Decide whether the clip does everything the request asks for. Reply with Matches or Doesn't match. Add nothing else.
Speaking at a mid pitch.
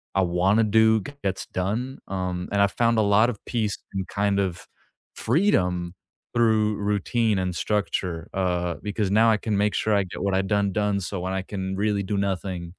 Doesn't match